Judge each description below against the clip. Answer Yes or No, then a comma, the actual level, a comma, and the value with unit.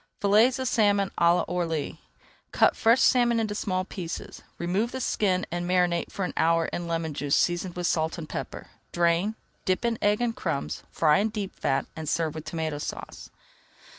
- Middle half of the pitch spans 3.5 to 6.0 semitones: Yes, average, 4.0 semitones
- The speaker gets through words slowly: No, average, 180 wpm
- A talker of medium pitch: Yes, medium, 180 Hz